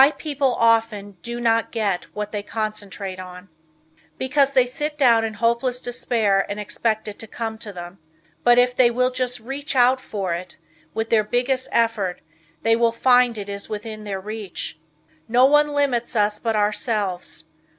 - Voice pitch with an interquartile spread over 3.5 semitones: No, average, 3.2 semitones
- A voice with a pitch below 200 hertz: No, high, 225 Hz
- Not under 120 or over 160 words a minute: No, average, 170 wpm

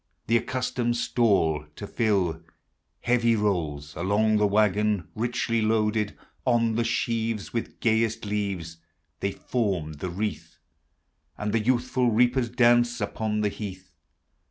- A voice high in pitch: No, low, 110 Hz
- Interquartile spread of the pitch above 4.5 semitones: No, average, 2.8 semitones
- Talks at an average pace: No, slow, 130 wpm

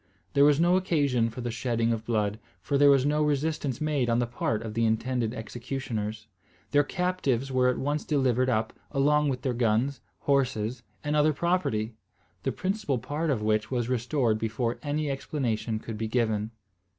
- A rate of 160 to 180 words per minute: Yes, average, 175 wpm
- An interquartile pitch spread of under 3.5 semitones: No, average, 4.2 semitones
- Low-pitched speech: Yes, low, 125 Hz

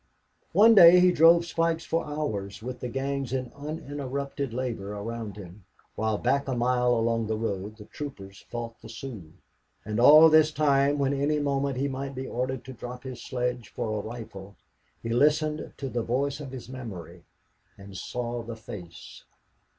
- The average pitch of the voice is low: Yes, low, 125 Hz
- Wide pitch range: No, average, 3.9 semitones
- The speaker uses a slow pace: No, average, 175 wpm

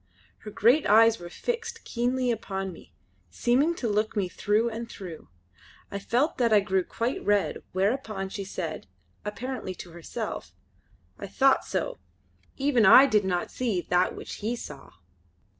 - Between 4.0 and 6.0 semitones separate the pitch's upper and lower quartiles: Yes, average, 4.5 semitones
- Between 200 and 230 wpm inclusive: No, average, 155 wpm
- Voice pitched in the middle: No, high, 215 Hz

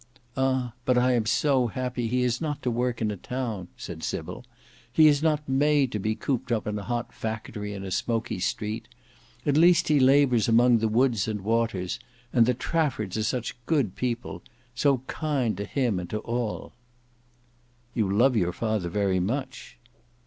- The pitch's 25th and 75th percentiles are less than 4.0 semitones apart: Yes, average, 3.6 semitones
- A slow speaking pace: No, average, 185 wpm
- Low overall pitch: Yes, low, 120 Hz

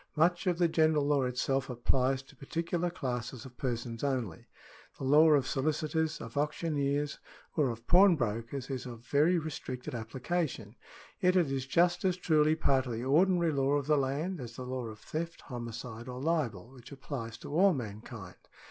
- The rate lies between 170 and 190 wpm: Yes, average, 180 wpm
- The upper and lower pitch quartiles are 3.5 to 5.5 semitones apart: Yes, average, 4.4 semitones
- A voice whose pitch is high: No, low, 135 Hz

